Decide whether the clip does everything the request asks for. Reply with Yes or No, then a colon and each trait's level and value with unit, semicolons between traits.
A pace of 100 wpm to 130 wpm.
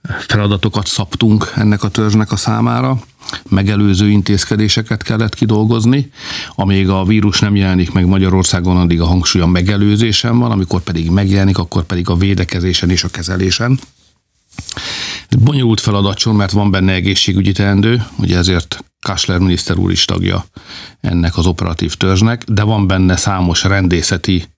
No: average, 140 wpm